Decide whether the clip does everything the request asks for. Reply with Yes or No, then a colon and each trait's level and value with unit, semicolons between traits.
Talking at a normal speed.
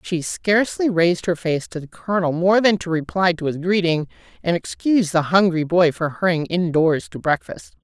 Yes: average, 190 wpm